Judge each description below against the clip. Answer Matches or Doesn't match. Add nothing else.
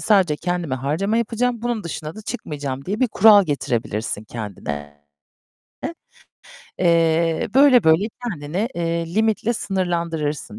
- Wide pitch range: Matches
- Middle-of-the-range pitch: Matches